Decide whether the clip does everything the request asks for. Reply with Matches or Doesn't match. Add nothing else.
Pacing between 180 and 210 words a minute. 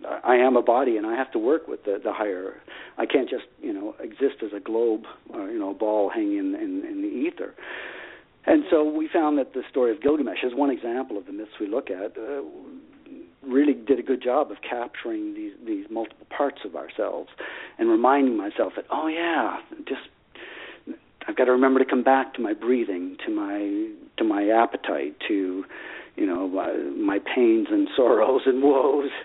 Matches